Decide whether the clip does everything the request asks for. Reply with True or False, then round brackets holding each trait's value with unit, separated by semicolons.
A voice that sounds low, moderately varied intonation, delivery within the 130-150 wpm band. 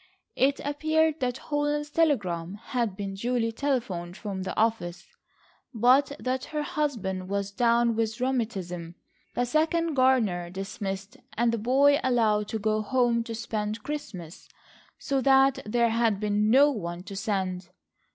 False (230 Hz; 5.0 semitones; 140 wpm)